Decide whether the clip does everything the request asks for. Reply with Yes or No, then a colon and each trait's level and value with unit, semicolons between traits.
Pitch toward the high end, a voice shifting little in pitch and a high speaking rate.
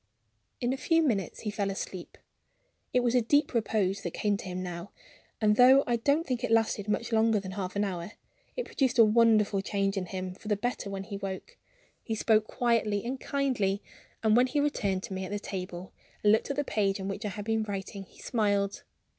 No: high, 210 Hz; average, 3.3 semitones; fast, 220 wpm